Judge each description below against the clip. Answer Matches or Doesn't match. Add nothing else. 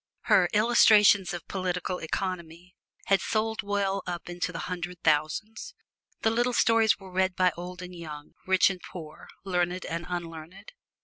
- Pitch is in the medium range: Matches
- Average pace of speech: Matches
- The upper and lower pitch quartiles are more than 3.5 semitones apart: Doesn't match